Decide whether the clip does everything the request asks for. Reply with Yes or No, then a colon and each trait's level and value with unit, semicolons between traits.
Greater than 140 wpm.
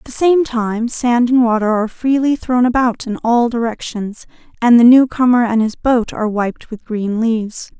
Yes: average, 195 wpm